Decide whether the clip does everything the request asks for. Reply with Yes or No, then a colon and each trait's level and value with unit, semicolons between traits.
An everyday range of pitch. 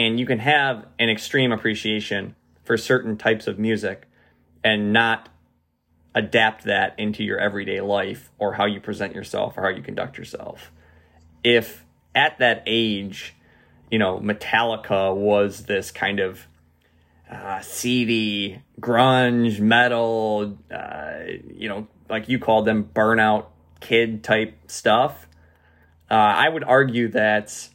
Yes: average, 3.3 semitones